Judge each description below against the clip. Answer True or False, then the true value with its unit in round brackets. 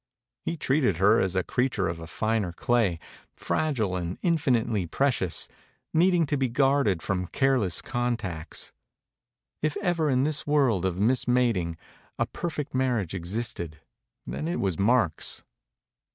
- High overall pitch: False (120 Hz)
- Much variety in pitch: True (7.0 semitones)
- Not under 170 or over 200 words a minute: False (155 wpm)